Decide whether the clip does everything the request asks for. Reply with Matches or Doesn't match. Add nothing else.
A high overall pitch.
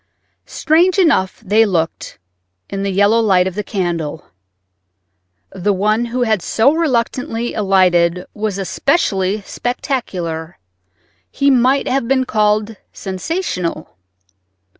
Matches